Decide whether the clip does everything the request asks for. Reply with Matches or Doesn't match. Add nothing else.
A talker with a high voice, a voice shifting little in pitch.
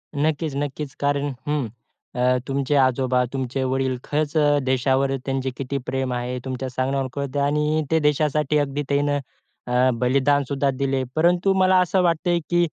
Doesn't match